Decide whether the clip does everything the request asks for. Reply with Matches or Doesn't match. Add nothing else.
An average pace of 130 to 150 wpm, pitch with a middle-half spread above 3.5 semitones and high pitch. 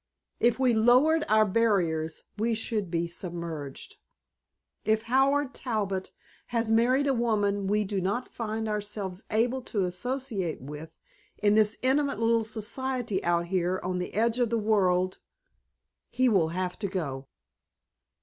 Matches